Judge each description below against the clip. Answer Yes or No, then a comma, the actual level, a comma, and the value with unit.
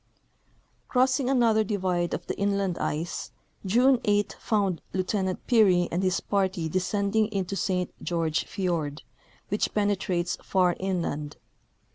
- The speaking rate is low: Yes, slow, 125 wpm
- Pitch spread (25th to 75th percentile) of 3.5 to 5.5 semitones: No, average, 2.8 semitones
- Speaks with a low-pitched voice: No, high, 190 Hz